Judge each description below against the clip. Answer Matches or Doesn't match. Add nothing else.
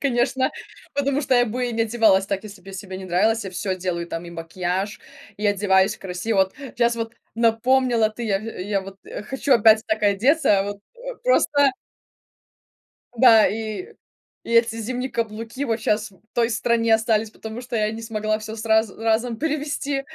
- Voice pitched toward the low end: Doesn't match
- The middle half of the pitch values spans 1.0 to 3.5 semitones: Matches